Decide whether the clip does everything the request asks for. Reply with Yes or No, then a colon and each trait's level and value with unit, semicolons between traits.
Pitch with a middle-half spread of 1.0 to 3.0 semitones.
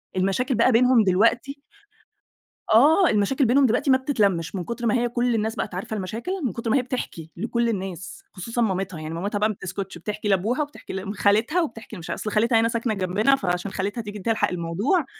No: average, 4.1 semitones